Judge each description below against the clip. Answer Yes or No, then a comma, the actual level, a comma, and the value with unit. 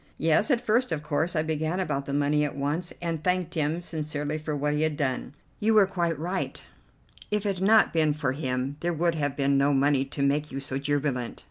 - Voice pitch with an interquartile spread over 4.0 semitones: No, average, 3.3 semitones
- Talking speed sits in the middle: No, fast, 225 wpm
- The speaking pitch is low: No, medium, 150 Hz